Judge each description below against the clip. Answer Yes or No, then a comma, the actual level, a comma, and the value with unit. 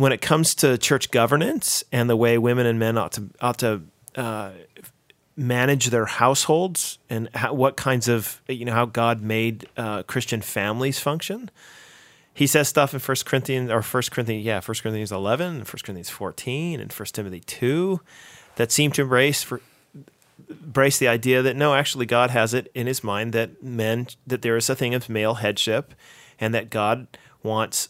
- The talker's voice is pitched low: Yes, low, 125 Hz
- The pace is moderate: Yes, average, 185 wpm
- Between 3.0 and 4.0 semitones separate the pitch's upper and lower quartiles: Yes, average, 3.4 semitones